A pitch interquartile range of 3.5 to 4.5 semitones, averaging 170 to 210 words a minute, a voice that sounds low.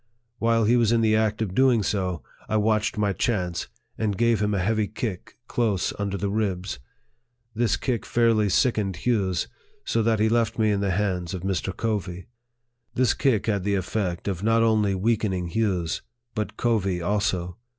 No: average, 3.1 semitones; average, 175 wpm; low, 105 Hz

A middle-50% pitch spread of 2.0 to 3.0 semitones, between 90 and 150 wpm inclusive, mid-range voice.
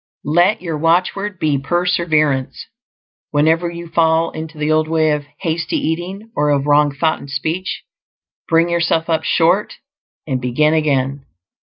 Yes: narrow, 2.4 semitones; average, 145 wpm; medium, 160 Hz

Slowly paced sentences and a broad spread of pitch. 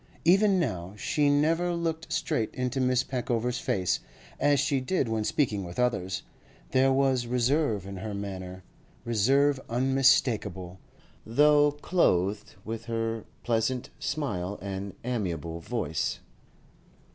Yes: slow, 120 wpm; wide, 5.7 semitones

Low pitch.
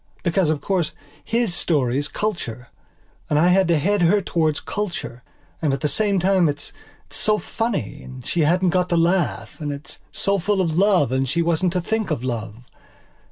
No: medium, 170 Hz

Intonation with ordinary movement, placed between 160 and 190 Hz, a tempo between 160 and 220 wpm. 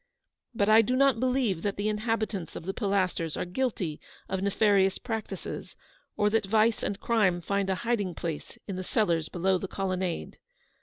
No: average, 3.1 semitones; high, 200 Hz; average, 170 wpm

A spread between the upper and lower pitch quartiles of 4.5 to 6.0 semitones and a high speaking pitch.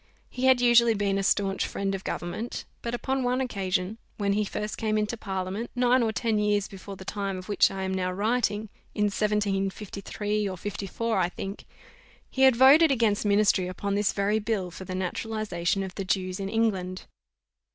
No: narrow, 2.6 semitones; high, 205 Hz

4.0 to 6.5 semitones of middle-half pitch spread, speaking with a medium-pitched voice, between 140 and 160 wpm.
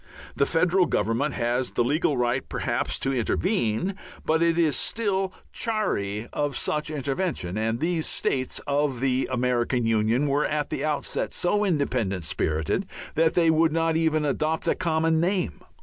Yes: average, 5.2 semitones; medium, 150 Hz; average, 155 wpm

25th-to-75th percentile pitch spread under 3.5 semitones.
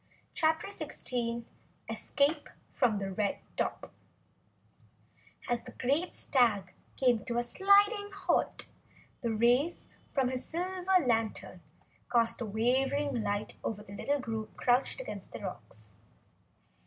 No: average, 5.1 semitones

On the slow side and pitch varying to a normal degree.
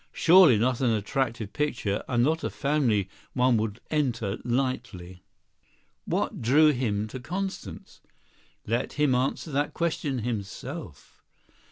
Yes: slow, 125 wpm; average, 5.0 semitones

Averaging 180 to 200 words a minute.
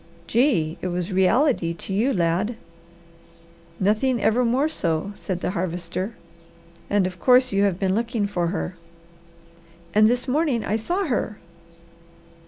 No: average, 140 wpm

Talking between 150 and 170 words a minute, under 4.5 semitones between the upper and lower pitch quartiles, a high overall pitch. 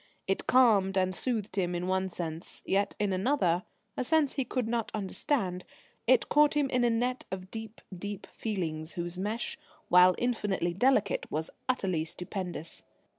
No: average, 160 wpm; average, 4.9 semitones; high, 195 Hz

